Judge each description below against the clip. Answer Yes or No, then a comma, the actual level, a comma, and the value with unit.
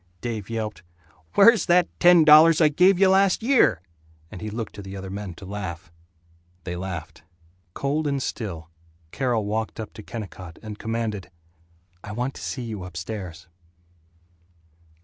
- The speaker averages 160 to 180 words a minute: No, average, 150 wpm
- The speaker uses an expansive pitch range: Yes, wide, 7.3 semitones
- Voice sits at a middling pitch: No, low, 110 Hz